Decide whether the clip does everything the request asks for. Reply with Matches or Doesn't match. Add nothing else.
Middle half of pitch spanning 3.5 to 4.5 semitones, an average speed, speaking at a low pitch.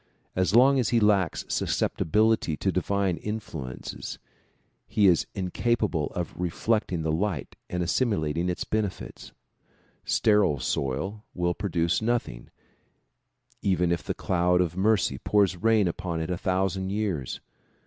Doesn't match